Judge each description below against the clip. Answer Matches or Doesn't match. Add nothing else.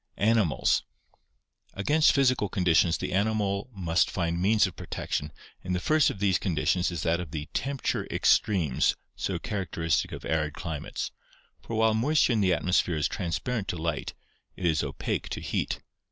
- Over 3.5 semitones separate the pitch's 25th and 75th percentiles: Matches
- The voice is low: Matches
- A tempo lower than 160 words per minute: Doesn't match